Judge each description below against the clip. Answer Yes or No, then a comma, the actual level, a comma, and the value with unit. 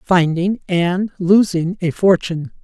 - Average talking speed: No, slow, 115 wpm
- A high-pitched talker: No, medium, 180 Hz